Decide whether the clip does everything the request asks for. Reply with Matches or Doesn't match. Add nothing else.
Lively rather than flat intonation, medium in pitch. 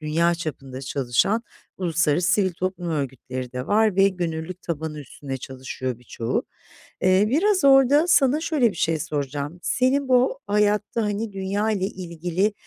Matches